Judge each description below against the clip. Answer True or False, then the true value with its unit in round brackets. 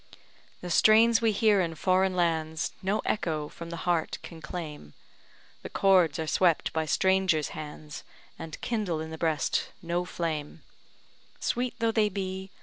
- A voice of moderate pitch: True (175 Hz)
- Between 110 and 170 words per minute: True (150 wpm)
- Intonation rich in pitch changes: False (3.3 semitones)